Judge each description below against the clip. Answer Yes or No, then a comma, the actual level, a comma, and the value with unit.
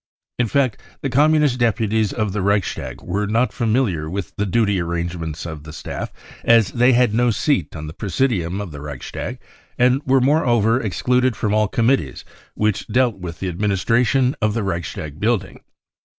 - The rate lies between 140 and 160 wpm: No, average, 180 wpm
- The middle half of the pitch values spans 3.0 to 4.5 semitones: No, wide, 5.5 semitones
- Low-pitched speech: Yes, low, 110 Hz